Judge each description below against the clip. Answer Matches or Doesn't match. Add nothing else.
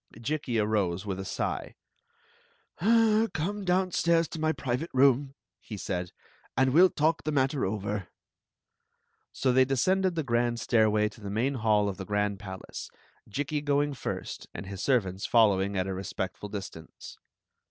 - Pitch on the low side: Matches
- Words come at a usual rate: Matches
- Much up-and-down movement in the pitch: Matches